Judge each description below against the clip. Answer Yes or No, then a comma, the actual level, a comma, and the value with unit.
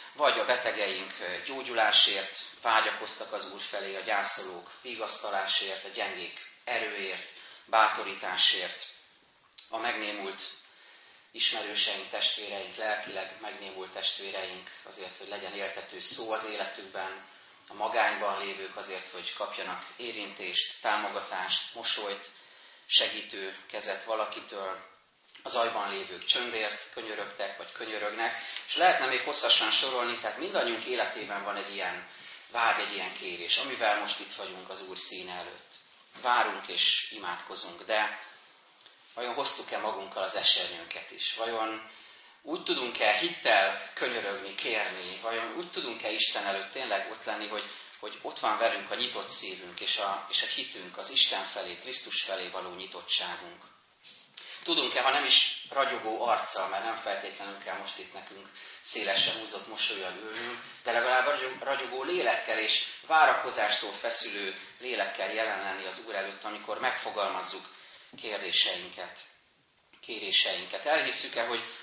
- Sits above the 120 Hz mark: No, low, 100 Hz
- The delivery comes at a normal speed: Yes, average, 125 wpm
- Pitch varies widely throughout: No, narrow, 2.5 semitones